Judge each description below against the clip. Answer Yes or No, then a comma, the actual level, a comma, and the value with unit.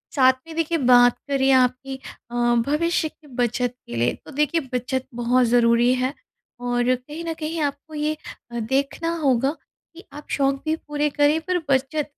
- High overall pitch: Yes, very high, 270 Hz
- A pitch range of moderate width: Yes, average, 3.4 semitones